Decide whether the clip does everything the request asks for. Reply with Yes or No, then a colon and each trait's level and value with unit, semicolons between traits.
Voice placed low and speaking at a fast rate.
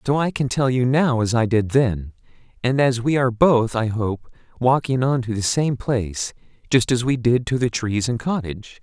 Yes: low, 125 Hz; fast, 220 wpm